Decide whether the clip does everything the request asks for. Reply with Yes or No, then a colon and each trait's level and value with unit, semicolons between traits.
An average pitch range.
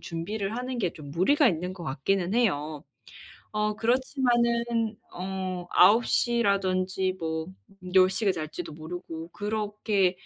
Yes: average, 4.2 semitones